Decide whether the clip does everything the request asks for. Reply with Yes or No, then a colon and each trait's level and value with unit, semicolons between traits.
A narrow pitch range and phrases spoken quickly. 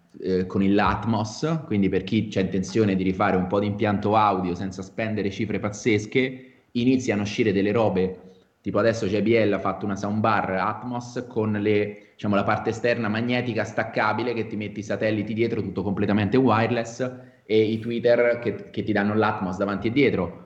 Yes: narrow, 2.3 semitones; fast, 175 wpm